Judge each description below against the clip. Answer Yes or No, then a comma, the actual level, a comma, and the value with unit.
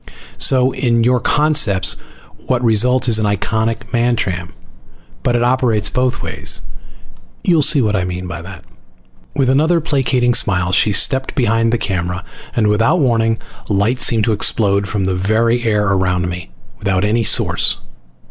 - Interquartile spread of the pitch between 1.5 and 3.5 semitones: No, average, 4.3 semitones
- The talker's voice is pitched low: Yes, low, 115 Hz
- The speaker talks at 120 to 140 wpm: No, average, 155 wpm